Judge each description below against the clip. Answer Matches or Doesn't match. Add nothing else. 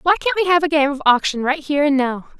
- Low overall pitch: Doesn't match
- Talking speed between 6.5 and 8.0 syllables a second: Matches